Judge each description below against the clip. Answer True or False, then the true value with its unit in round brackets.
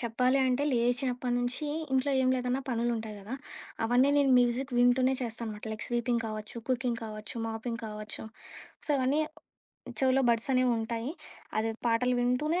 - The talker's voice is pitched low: False (245 Hz)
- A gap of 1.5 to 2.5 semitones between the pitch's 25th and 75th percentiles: True (2.1 semitones)